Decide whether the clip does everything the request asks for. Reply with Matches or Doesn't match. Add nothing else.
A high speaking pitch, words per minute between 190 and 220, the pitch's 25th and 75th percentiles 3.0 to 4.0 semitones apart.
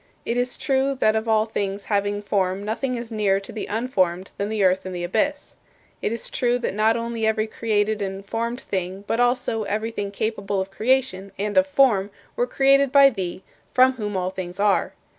Matches